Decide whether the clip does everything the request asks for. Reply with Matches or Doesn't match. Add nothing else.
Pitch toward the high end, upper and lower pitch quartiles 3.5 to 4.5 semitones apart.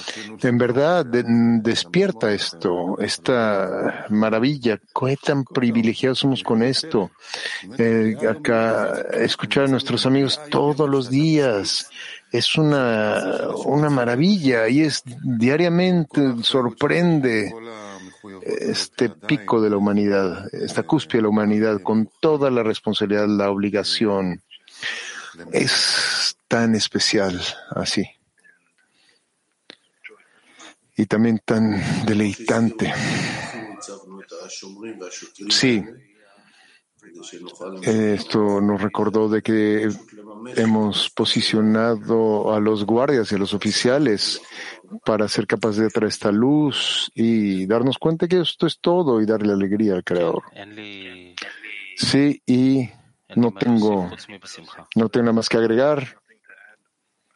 Doesn't match